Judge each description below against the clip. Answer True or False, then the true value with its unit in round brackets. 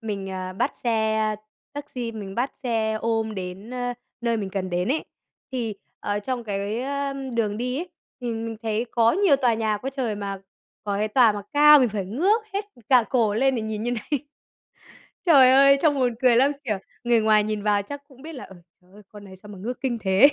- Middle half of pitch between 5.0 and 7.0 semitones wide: False (3.8 semitones)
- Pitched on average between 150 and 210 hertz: False (230 Hz)